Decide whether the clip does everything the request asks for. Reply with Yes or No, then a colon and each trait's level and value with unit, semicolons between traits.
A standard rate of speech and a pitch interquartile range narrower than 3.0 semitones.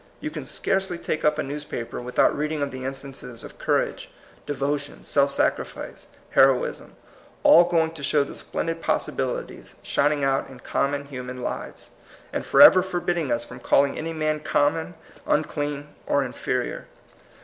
Yes: average, 155 wpm; narrow, 2.6 semitones